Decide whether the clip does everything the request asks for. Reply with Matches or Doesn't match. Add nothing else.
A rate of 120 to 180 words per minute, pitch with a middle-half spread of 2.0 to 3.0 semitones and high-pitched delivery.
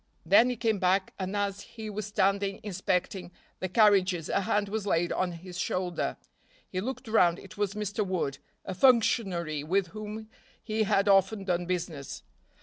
Matches